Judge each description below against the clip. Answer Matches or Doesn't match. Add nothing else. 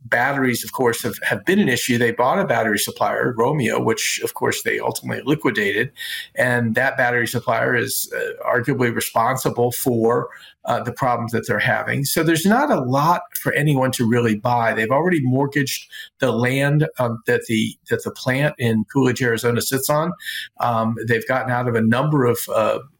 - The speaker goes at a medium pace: Matches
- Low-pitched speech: Matches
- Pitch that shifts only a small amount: Doesn't match